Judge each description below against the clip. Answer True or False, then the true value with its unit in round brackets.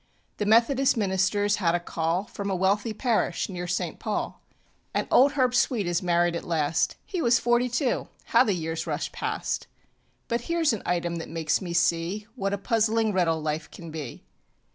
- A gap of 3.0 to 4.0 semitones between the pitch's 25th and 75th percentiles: False (5.1 semitones)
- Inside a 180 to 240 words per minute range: True (185 wpm)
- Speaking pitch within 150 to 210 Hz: True (190 Hz)